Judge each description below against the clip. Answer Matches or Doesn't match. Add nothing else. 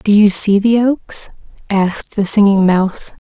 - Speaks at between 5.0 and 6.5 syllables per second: Doesn't match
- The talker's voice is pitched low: Doesn't match